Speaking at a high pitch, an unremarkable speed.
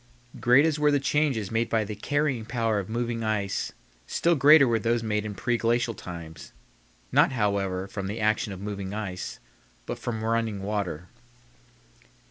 No: low, 110 Hz; average, 160 wpm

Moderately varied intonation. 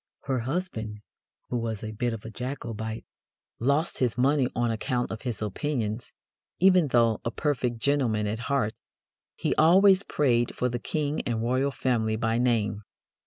Yes: average, 4.0 semitones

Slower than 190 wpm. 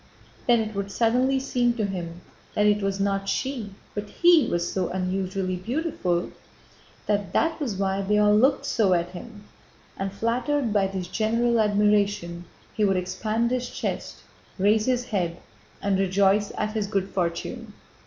Yes: average, 165 wpm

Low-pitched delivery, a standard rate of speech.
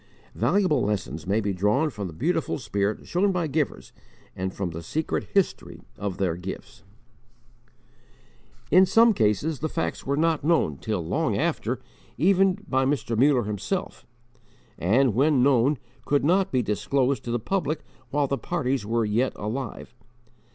Yes: low, 130 Hz; average, 150 wpm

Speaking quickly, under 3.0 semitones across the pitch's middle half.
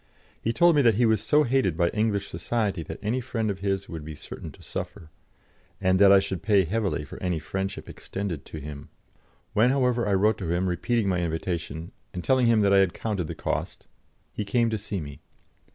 No: fast, 215 wpm; average, 4.3 semitones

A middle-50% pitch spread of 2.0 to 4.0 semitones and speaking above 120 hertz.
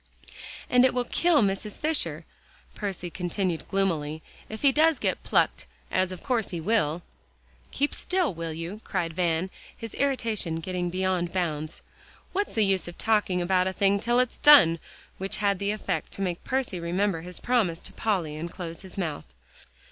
No: average, 4.6 semitones; high, 190 Hz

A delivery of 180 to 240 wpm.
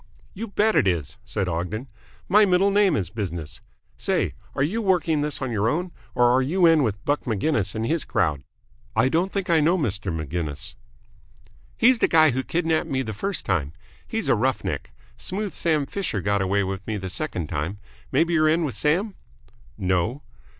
Yes: average, 190 wpm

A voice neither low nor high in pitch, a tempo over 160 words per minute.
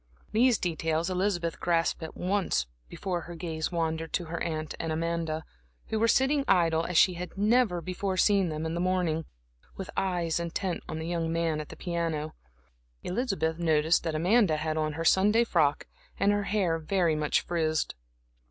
Yes: medium, 170 Hz; average, 175 wpm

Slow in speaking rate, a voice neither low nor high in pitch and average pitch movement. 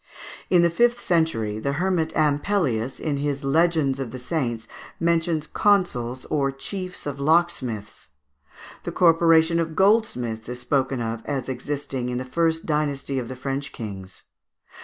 No: average, 145 wpm; medium, 145 Hz; average, 4.9 semitones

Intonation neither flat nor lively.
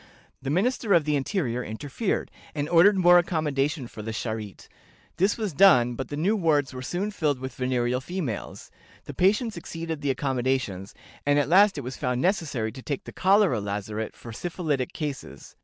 No: wide, 6.0 semitones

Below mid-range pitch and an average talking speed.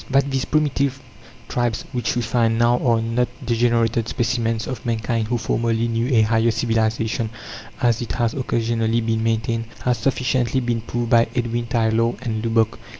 Yes: low, 115 Hz; average, 160 wpm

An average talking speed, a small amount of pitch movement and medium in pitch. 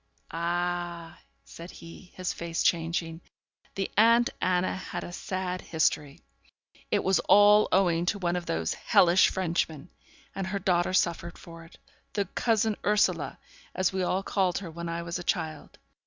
Yes: average, 155 wpm; narrow, 2.1 semitones; medium, 175 Hz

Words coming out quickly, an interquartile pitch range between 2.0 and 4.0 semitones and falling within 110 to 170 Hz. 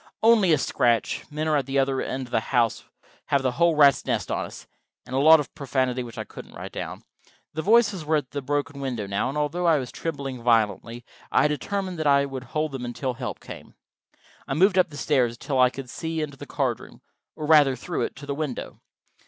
Yes: fast, 230 wpm; average, 3.5 semitones; medium, 140 Hz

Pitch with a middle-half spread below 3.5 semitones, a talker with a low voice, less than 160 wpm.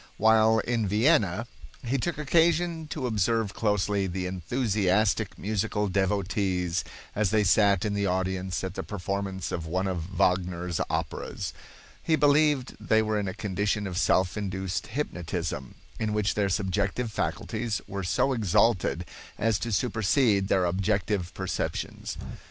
Yes: average, 3.0 semitones; low, 100 Hz; average, 140 wpm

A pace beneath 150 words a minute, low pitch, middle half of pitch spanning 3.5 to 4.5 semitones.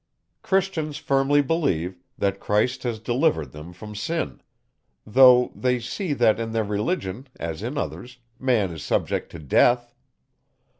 No: average, 140 wpm; low, 120 Hz; average, 5.3 semitones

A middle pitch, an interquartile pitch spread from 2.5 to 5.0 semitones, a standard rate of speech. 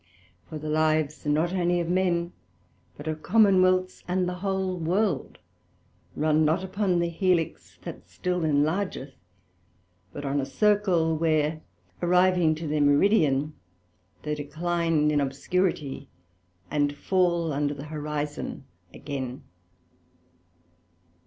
No: medium, 160 Hz; average, 3.5 semitones; slow, 115 wpm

